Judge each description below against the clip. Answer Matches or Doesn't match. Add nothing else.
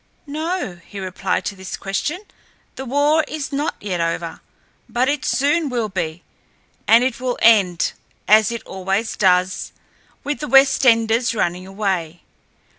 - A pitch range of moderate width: Doesn't match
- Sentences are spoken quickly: Doesn't match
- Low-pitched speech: Doesn't match